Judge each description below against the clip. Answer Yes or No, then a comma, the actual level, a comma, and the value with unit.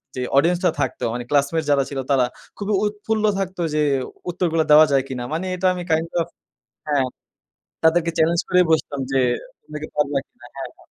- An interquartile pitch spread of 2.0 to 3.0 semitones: No, average, 4.0 semitones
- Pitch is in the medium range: Yes, medium, 160 Hz